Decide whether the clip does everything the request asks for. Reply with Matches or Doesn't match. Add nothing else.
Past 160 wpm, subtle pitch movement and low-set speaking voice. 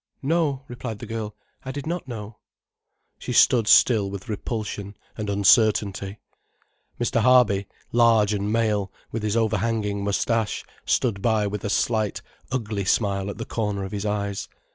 Doesn't match